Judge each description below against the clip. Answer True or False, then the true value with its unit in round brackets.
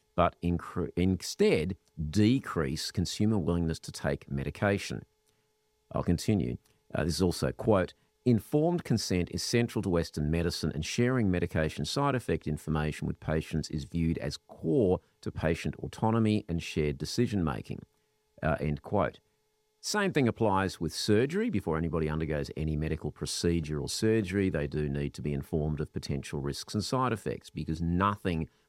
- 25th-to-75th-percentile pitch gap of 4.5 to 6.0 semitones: True (5.6 semitones)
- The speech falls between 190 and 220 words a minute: False (150 wpm)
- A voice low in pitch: True (85 Hz)